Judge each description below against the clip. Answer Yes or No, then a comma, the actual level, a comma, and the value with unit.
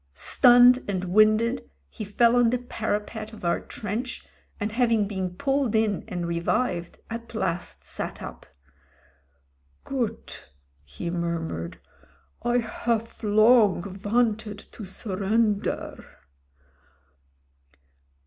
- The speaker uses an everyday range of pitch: Yes, average, 3.9 semitones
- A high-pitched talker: Yes, high, 215 Hz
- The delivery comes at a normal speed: No, slow, 105 wpm